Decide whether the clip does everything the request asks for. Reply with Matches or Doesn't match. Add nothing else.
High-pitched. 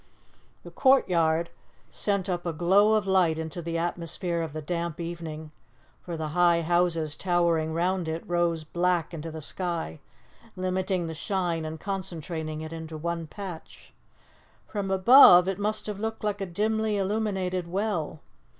Doesn't match